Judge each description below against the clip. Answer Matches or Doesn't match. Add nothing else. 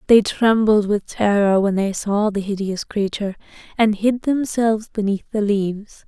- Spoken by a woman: Matches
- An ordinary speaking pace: Matches